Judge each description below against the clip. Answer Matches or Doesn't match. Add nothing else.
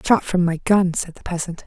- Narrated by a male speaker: Doesn't match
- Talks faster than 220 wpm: Matches